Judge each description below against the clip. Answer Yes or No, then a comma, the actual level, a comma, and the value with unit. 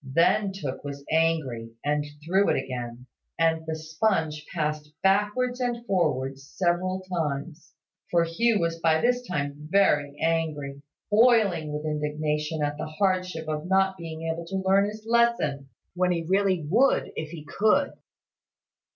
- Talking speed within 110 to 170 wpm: Yes, average, 145 wpm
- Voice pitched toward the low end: No, medium, 165 Hz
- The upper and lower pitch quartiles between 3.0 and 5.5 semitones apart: Yes, average, 4.3 semitones